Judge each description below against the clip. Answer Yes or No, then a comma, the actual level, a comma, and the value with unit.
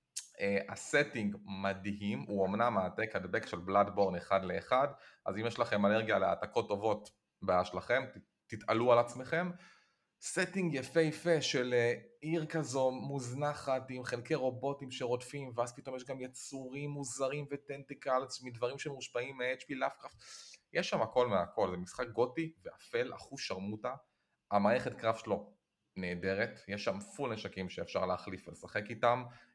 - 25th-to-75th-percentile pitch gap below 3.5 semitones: No, wide, 5.4 semitones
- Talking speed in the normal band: Yes, average, 140 wpm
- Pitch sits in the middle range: No, low, 125 Hz